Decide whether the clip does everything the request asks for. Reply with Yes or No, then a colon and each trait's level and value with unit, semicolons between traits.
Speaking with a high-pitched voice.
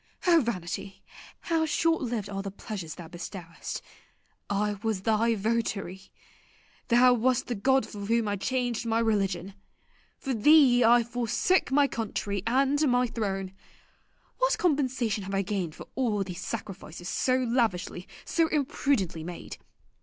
Yes: high, 225 Hz